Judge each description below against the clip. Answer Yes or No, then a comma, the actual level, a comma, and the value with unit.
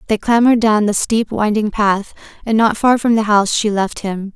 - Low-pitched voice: No, high, 215 Hz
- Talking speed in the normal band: No, fast, 220 wpm